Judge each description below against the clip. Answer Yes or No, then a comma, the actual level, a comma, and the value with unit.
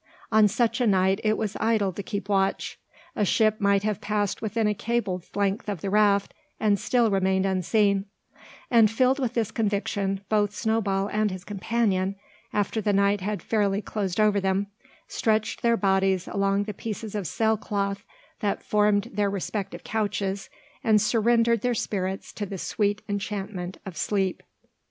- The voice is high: Yes, high, 205 Hz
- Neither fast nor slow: Yes, average, 165 wpm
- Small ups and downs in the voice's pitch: Yes, narrow, 1.9 semitones